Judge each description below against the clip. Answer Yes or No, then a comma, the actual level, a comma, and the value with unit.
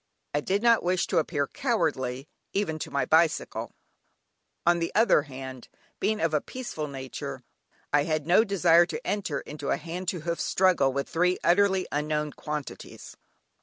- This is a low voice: No, medium, 165 Hz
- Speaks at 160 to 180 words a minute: Yes, average, 165 wpm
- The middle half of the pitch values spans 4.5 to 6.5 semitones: No, average, 4.0 semitones